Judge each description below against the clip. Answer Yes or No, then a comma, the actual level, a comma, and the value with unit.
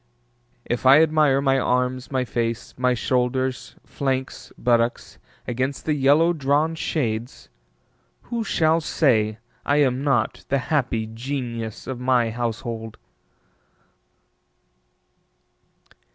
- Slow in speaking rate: Yes, slow, 105 wpm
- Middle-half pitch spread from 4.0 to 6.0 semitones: No, average, 3.1 semitones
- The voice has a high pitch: No, low, 130 Hz